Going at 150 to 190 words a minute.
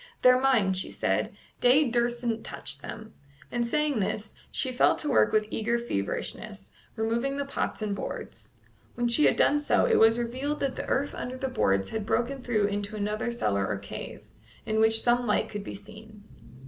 Yes: average, 185 wpm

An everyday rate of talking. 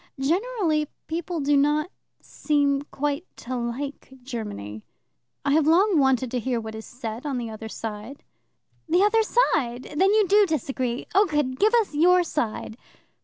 Yes: average, 160 wpm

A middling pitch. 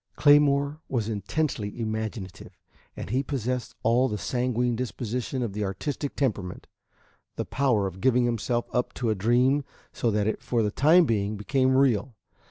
No: low, 120 Hz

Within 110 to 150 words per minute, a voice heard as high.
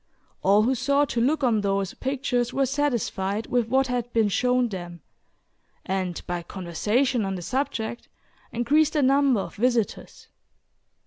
Yes: average, 145 wpm; high, 240 Hz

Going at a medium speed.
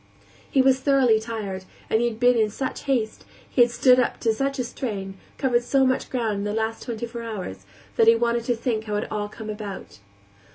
No: fast, 220 wpm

